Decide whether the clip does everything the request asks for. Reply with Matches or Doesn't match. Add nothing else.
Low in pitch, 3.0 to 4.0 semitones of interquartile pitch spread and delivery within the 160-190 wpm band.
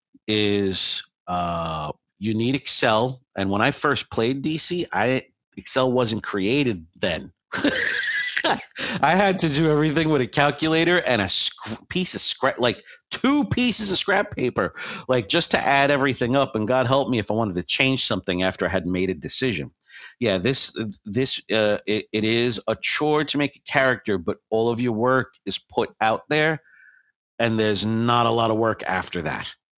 Doesn't match